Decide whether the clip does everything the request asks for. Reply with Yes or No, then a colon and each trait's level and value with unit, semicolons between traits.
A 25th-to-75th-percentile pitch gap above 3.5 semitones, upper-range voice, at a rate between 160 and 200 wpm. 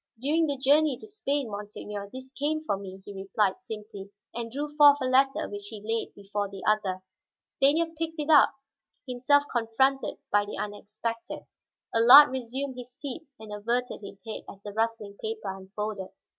Yes: average, 5.1 semitones; high, 230 Hz; average, 170 wpm